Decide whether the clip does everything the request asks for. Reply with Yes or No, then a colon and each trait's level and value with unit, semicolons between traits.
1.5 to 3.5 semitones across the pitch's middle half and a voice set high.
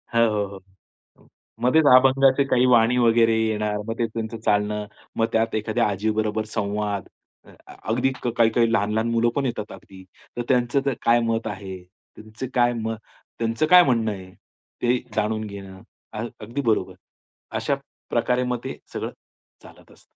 No: narrow, 2.4 semitones; low, 115 Hz